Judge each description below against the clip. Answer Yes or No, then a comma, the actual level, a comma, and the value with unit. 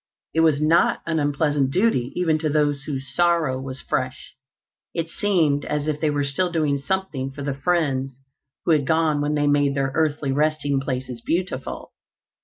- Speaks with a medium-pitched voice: Yes, medium, 145 Hz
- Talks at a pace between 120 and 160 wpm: No, average, 175 wpm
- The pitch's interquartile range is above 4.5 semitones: No, average, 2.8 semitones